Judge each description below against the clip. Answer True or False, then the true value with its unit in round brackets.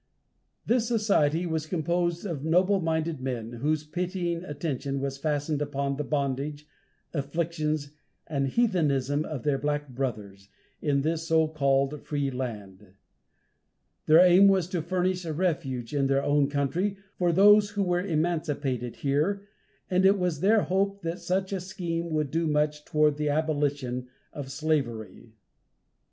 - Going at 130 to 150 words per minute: True (145 wpm)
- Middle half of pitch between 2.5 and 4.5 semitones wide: True (4.1 semitones)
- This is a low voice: False (155 Hz)